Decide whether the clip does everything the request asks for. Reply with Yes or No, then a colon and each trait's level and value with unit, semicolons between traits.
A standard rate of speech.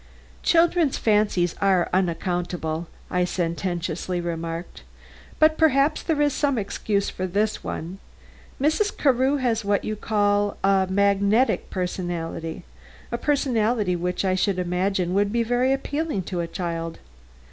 No: slow, 125 wpm